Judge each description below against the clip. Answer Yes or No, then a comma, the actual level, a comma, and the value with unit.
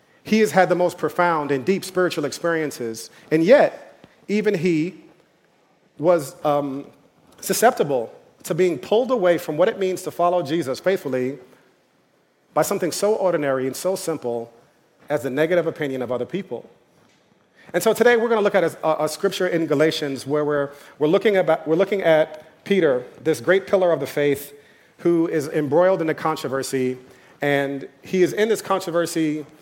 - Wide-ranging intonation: No, average, 4.2 semitones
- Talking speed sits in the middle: Yes, average, 170 wpm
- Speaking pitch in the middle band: Yes, medium, 165 Hz